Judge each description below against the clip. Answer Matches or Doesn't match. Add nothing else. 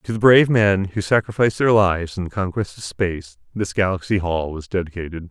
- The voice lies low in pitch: Matches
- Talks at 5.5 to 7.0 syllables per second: Matches